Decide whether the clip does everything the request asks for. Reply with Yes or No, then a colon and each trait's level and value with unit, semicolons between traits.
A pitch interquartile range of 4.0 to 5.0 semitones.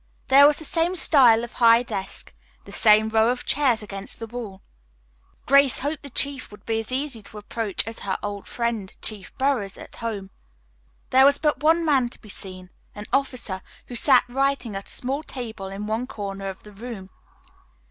Yes: average, 4.7 semitones